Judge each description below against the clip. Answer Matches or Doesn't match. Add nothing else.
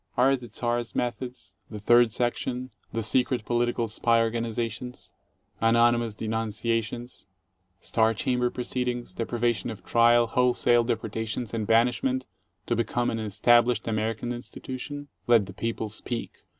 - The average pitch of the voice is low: Matches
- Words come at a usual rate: Doesn't match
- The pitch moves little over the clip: Matches